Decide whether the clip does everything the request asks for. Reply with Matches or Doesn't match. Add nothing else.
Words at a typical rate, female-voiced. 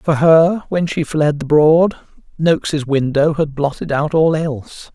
Doesn't match